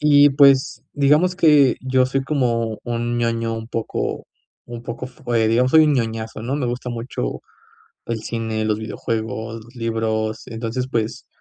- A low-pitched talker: Yes, low, 120 Hz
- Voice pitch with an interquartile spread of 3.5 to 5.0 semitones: No, average, 2.7 semitones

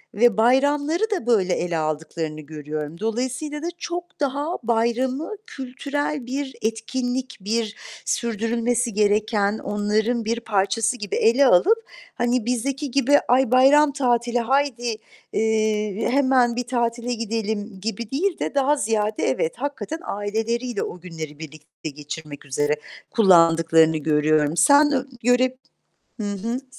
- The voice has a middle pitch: No, high, 230 Hz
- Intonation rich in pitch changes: No, average, 4.5 semitones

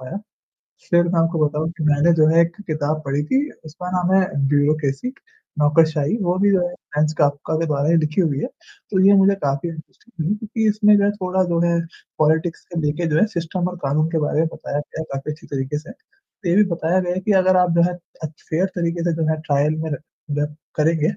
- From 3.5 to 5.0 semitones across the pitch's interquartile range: No, average, 3.1 semitones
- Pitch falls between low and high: Yes, medium, 165 Hz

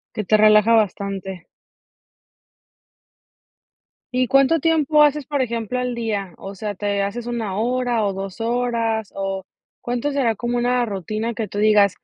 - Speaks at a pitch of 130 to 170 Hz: No, high, 225 Hz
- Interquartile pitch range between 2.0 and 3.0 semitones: No, average, 3.4 semitones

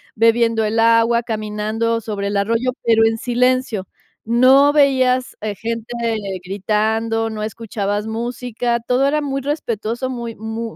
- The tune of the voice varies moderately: No, narrow, 2.2 semitones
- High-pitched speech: Yes, high, 230 Hz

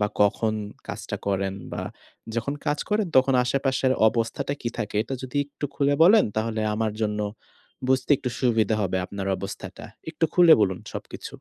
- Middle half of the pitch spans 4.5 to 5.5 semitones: Yes, average, 4.8 semitones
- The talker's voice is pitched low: Yes, low, 115 Hz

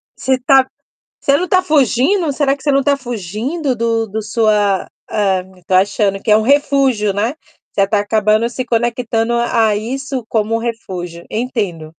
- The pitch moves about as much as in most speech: Yes, average, 4.2 semitones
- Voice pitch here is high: Yes, high, 230 Hz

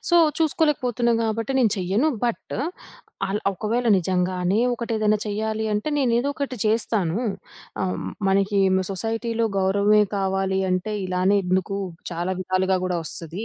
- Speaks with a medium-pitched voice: No, high, 205 Hz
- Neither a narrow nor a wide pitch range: Yes, average, 3.4 semitones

